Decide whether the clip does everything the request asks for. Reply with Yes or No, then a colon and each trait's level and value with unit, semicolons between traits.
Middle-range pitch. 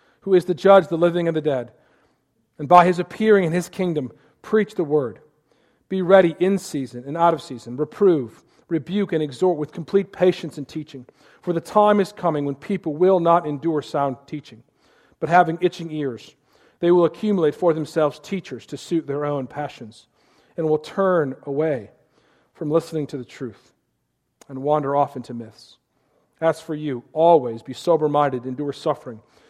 Yes: medium, 155 Hz